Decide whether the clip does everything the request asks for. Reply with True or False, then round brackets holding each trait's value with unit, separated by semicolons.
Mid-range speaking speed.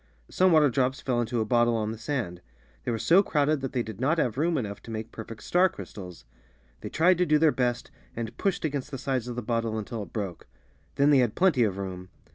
False (245 wpm)